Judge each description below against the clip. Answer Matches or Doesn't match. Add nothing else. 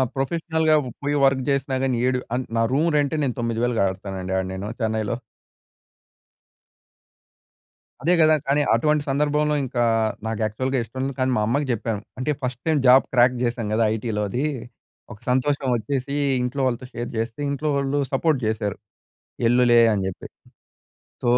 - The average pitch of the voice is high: Doesn't match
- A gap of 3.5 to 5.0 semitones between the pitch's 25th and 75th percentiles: Matches